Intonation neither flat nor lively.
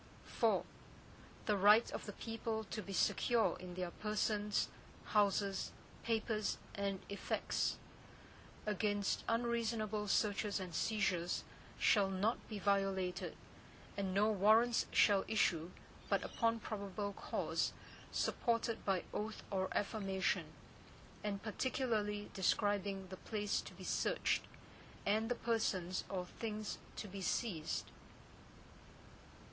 No: narrow, 2.1 semitones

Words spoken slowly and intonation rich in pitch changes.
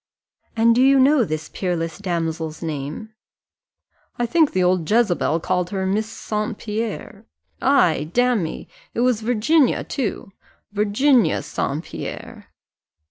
Yes: slow, 125 wpm; wide, 6.1 semitones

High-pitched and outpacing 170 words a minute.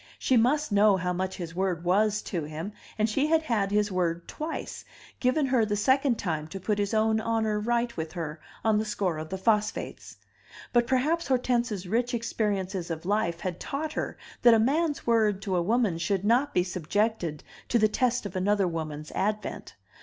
Yes: high, 210 Hz; average, 190 wpm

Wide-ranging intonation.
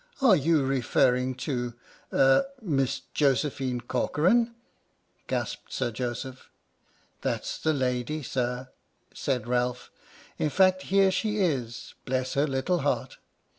No: average, 4.8 semitones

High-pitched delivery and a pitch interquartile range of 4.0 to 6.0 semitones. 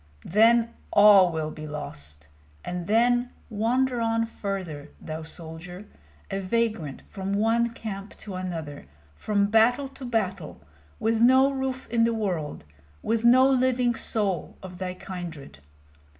Yes: high, 205 Hz; average, 5.0 semitones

